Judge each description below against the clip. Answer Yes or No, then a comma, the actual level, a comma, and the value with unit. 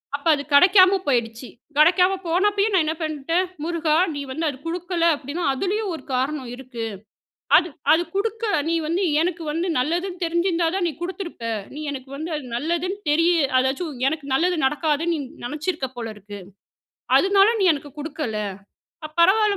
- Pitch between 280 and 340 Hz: Yes, very high, 330 Hz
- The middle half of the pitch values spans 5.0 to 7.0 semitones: No, average, 4.3 semitones